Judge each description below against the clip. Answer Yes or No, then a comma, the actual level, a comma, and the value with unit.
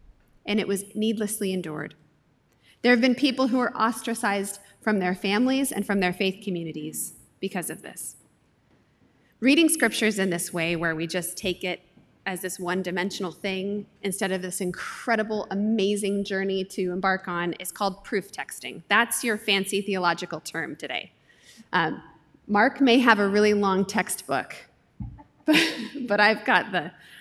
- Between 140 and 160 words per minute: Yes, average, 155 wpm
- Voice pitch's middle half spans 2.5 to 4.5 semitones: Yes, average, 3.1 semitones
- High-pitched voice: Yes, high, 195 Hz